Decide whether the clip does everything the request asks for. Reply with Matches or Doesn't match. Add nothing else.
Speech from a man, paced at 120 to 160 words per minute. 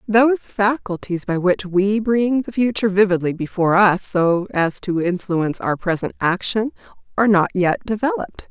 Doesn't match